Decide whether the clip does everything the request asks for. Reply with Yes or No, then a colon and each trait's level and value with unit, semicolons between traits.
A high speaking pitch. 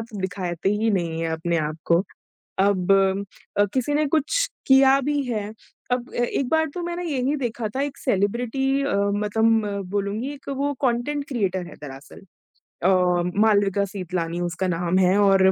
Yes: high, 210 Hz